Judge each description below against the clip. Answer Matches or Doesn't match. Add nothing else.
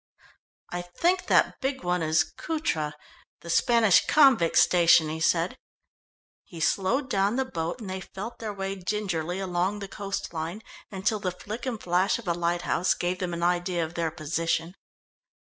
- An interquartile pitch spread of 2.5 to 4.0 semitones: Matches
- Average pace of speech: Matches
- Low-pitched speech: Doesn't match